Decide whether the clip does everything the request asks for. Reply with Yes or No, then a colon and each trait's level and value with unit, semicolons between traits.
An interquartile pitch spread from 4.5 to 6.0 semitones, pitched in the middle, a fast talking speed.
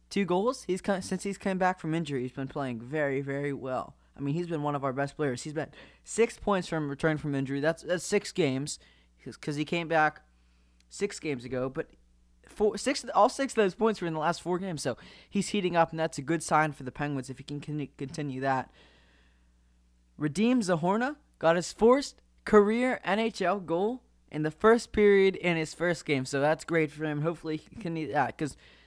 Yes: wide, 5.6 semitones; medium, 155 Hz; fast, 210 wpm